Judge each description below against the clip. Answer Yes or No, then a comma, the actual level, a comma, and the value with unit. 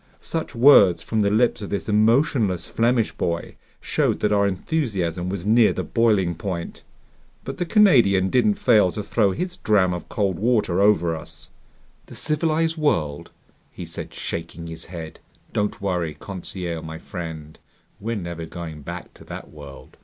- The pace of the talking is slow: No, average, 160 wpm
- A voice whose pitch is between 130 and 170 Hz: No, low, 100 Hz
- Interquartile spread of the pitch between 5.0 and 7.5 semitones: Yes, wide, 5.4 semitones